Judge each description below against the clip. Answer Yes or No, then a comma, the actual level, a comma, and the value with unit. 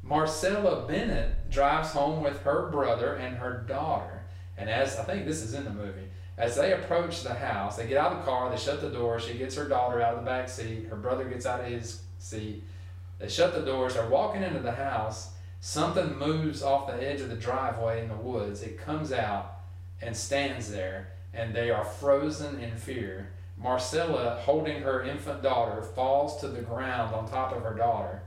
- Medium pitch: No, low, 115 Hz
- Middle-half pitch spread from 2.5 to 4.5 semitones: No, wide, 5.5 semitones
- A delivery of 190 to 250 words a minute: Yes, fast, 205 wpm